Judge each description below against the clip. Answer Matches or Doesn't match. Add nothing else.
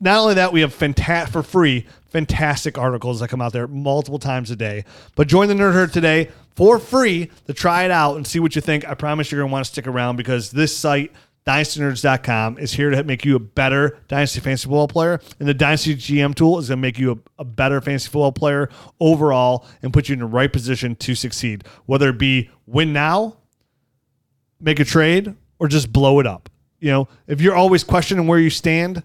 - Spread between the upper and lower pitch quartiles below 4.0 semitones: Matches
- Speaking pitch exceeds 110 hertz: Matches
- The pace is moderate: Doesn't match